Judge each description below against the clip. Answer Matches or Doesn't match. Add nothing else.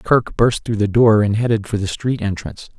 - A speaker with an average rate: Doesn't match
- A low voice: Matches